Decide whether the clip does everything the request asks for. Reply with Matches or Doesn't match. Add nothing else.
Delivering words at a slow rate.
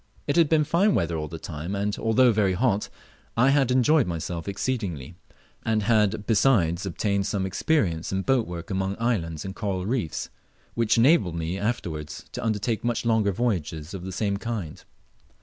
Doesn't match